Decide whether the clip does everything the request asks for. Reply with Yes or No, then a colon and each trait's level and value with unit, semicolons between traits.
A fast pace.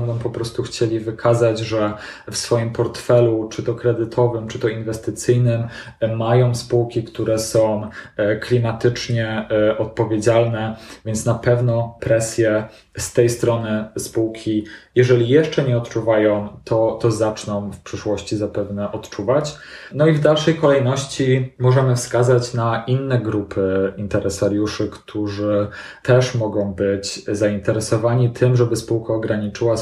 No: average, 120 wpm